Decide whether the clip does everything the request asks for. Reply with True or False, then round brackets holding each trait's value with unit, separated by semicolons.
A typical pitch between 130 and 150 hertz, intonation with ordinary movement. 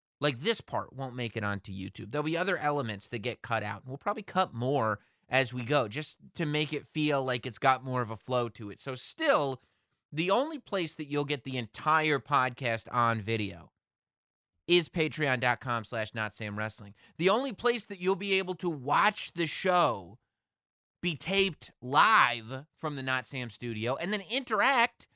False (135 Hz; 6.6 semitones)